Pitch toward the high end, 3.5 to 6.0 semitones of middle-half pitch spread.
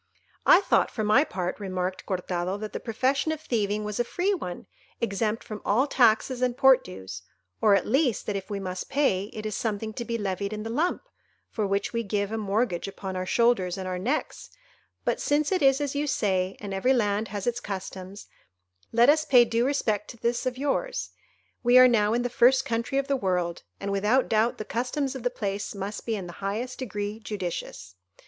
Yes: high, 215 Hz; average, 4.2 semitones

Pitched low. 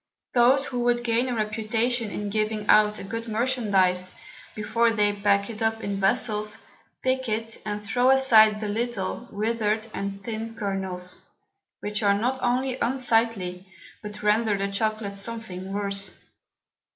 No: high, 215 Hz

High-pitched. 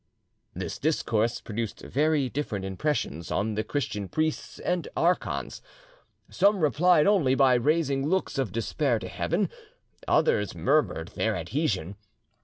No: low, 135 Hz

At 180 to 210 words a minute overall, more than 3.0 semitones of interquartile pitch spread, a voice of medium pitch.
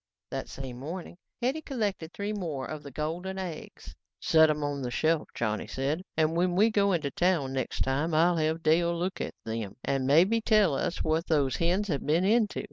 Yes: average, 200 wpm; average, 4.7 semitones; medium, 160 Hz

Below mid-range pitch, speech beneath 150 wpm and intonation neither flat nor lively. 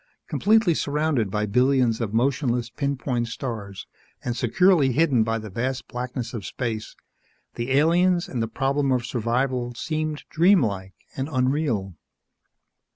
Yes: low, 125 Hz; average, 140 wpm; average, 4.0 semitones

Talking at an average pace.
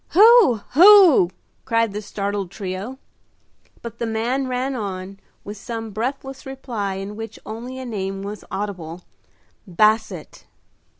No: slow, 125 wpm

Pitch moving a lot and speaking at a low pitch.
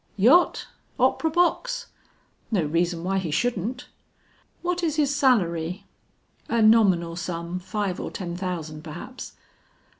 No: wide, 7.2 semitones; high, 190 Hz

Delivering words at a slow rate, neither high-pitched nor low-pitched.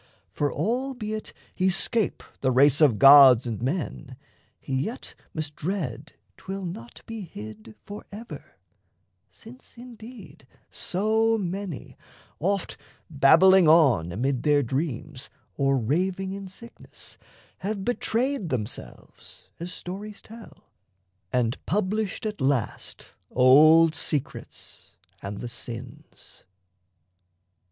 Yes: slow, 105 wpm; medium, 165 Hz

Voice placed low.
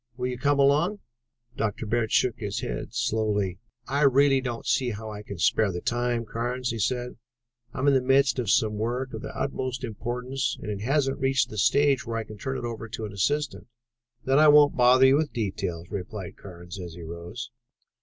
Yes: low, 120 Hz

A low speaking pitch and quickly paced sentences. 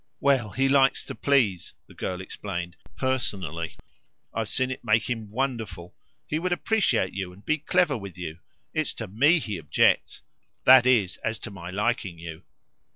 No: low, 110 Hz; average, 165 wpm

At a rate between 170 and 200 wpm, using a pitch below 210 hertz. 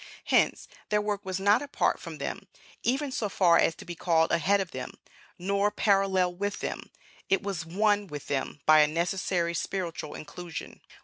Yes: average, 175 wpm; medium, 185 Hz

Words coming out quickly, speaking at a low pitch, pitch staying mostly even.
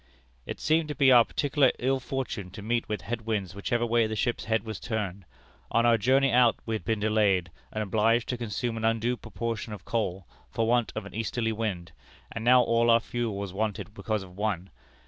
Yes: fast, 210 wpm; low, 115 Hz; narrow, 2.3 semitones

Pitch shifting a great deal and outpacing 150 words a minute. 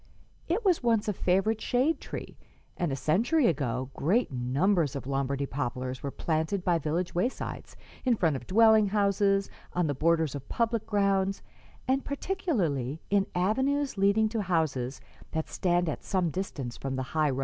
Yes: wide, 7.4 semitones; average, 165 wpm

